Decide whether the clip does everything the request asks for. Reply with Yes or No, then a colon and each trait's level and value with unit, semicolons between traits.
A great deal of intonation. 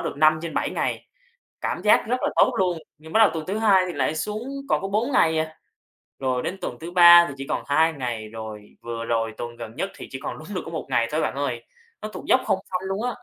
Yes: wide, 7.1 semitones